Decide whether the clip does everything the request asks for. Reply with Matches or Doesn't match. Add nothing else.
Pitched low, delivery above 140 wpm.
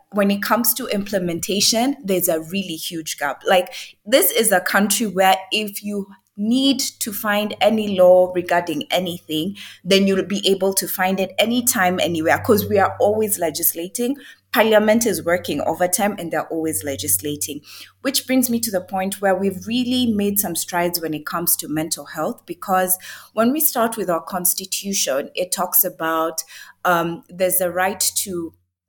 Doesn't match